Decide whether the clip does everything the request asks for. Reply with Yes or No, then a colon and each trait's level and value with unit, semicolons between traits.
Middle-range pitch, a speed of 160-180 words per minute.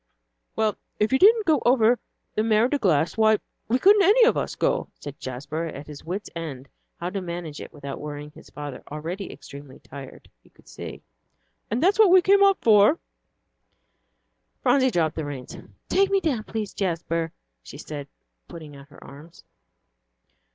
Yes: medium, 180 Hz; average, 175 wpm